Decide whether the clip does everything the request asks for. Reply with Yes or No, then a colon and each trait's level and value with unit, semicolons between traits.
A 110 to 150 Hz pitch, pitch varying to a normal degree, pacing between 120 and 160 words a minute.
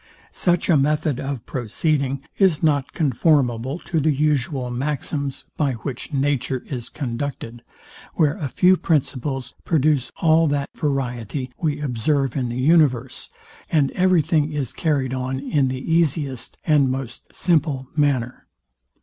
Yes: medium, 140 Hz; average, 3.0 semitones; slow, 135 wpm